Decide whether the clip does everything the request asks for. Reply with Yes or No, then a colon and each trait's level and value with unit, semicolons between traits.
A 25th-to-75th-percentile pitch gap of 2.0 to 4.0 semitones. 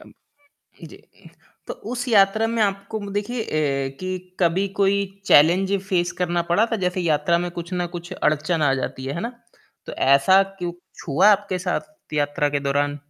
No: average, 4.8 semitones